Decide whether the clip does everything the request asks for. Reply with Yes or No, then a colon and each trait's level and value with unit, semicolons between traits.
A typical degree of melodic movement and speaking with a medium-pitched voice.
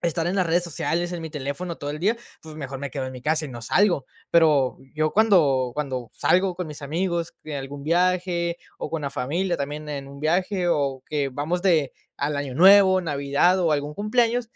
Yes: average, 4.1 semitones; medium, 155 Hz